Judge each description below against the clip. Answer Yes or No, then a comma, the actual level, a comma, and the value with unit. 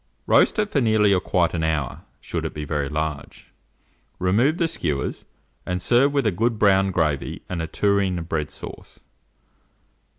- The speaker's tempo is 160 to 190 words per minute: Yes, average, 170 wpm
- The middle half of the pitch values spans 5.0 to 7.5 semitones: Yes, wide, 5.4 semitones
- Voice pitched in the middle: No, very low, 90 Hz